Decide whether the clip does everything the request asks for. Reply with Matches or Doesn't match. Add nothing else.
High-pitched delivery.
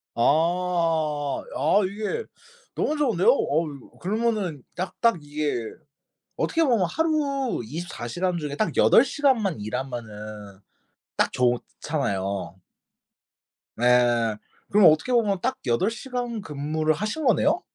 Doesn't match